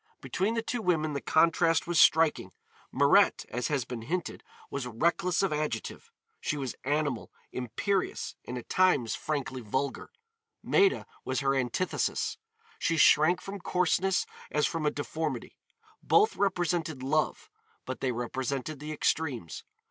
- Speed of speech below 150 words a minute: Yes, average, 140 wpm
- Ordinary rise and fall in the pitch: Yes, average, 5.0 semitones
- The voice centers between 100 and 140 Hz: No, medium, 155 Hz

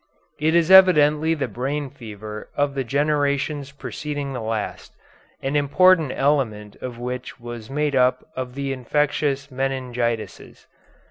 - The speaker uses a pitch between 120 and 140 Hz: Yes, low, 135 Hz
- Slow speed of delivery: Yes, slow, 130 wpm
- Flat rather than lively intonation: No, average, 3.0 semitones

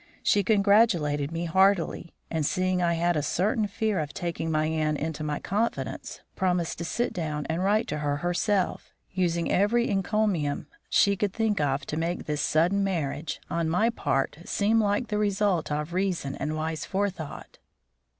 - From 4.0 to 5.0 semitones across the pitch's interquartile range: Yes, average, 4.5 semitones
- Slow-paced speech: No, average, 170 wpm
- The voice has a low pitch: No, medium, 175 Hz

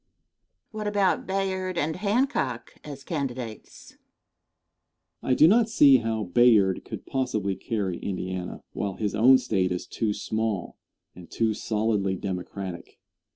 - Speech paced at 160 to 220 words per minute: No, slow, 135 wpm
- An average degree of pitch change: No, wide, 7.1 semitones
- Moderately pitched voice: No, low, 115 Hz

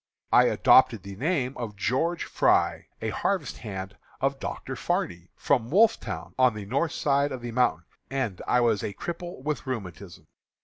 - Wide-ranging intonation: Yes, wide, 5.8 semitones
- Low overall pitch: Yes, low, 125 Hz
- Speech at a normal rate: Yes, average, 165 wpm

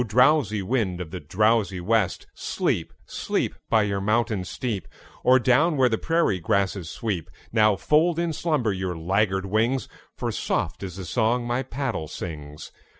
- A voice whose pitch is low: Yes, low, 110 Hz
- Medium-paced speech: Yes, average, 155 wpm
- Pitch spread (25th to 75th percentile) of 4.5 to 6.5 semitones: Yes, average, 5.1 semitones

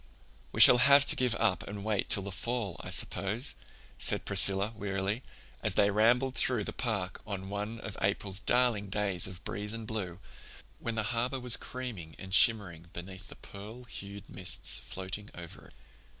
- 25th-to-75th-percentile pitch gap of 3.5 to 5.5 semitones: No, average, 3.1 semitones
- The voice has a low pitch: Yes, low, 105 Hz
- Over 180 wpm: No, average, 175 wpm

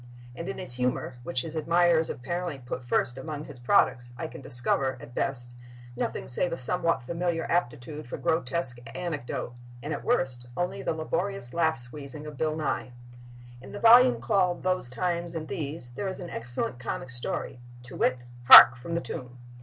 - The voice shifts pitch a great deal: Yes, wide, 5.7 semitones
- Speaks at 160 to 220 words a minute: Yes, average, 175 wpm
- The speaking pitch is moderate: Yes, medium, 150 Hz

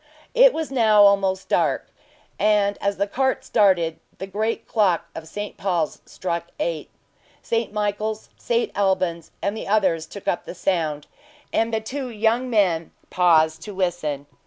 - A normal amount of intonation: Yes, average, 4.2 semitones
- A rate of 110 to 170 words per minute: Yes, average, 155 wpm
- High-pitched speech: Yes, high, 200 Hz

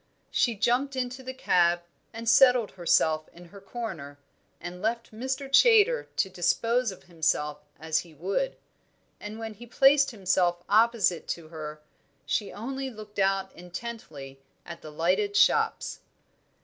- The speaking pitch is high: Yes, high, 200 Hz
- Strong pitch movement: Yes, wide, 5.8 semitones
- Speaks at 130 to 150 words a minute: Yes, average, 140 wpm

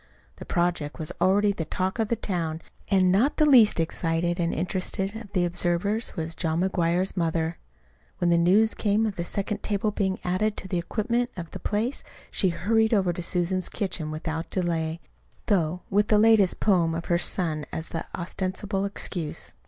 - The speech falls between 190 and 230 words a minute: No, average, 180 wpm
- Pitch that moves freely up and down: No, average, 3.4 semitones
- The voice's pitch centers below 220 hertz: Yes, medium, 185 Hz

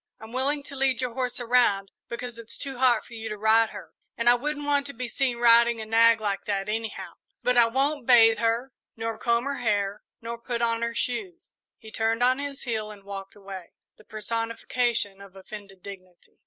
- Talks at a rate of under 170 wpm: No, fast, 205 wpm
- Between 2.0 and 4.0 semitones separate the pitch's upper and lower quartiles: Yes, average, 2.7 semitones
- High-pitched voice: Yes, high, 230 Hz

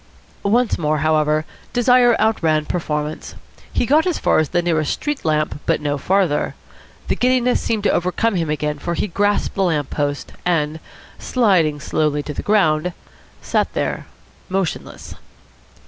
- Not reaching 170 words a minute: Yes, average, 150 wpm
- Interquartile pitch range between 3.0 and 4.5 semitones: No, wide, 5.6 semitones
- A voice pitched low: No, medium, 165 Hz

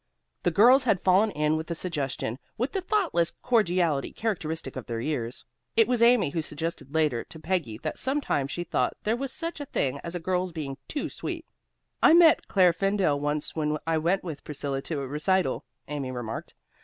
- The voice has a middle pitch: Yes, medium, 165 Hz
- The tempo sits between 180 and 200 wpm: Yes, average, 190 wpm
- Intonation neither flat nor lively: No, wide, 6.2 semitones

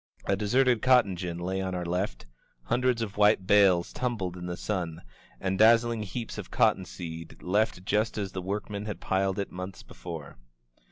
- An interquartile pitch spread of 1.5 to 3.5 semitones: Yes, average, 3.1 semitones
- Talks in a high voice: No, very low, 95 Hz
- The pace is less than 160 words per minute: No, average, 175 wpm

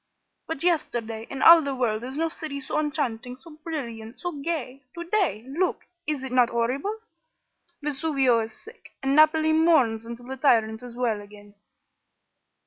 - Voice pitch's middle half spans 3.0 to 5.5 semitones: Yes, average, 5.1 semitones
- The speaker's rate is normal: Yes, average, 160 wpm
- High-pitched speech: Yes, very high, 265 Hz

